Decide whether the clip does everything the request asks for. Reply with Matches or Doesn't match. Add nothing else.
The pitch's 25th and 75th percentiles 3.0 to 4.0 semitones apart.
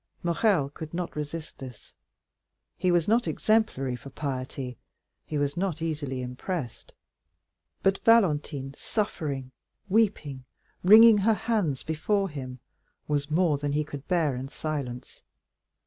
Doesn't match